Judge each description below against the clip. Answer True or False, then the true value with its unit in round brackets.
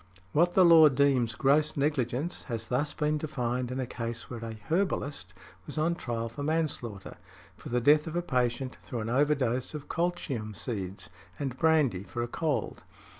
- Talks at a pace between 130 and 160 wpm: False (175 wpm)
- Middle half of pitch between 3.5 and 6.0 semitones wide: True (4.5 semitones)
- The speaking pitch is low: True (130 Hz)